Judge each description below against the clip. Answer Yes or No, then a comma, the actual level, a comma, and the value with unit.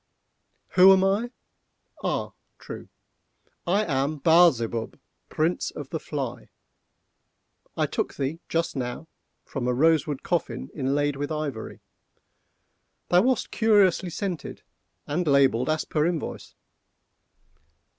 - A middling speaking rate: No, slow, 115 wpm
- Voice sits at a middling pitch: Yes, medium, 155 Hz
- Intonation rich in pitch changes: No, average, 4.5 semitones